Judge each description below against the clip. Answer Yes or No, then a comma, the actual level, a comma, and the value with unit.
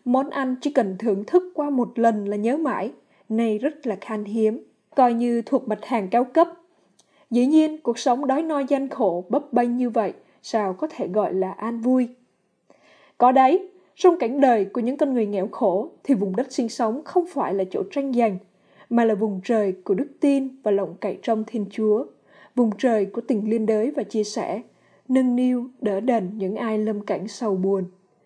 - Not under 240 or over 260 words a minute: No, average, 205 wpm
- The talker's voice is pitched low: No, high, 235 Hz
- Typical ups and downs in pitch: Yes, average, 4.0 semitones